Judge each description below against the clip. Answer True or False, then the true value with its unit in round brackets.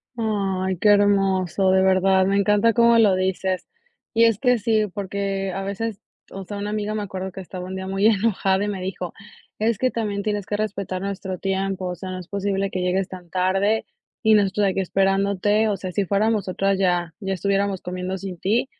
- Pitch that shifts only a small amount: True (1.6 semitones)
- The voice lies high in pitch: True (195 Hz)